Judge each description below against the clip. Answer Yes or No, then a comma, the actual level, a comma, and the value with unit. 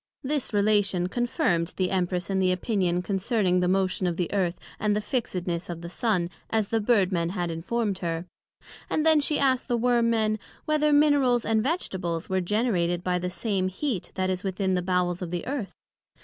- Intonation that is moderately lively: Yes, average, 4.5 semitones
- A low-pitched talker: No, high, 190 Hz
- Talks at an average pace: Yes, average, 190 wpm